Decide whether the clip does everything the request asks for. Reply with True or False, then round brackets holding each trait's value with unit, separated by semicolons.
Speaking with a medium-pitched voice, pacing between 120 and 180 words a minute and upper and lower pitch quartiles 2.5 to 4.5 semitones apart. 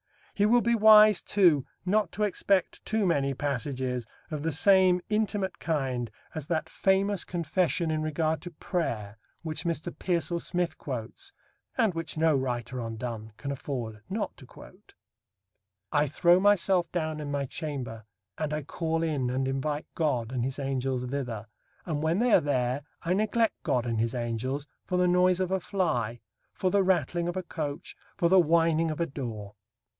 False (155 Hz; 175 wpm; 5.6 semitones)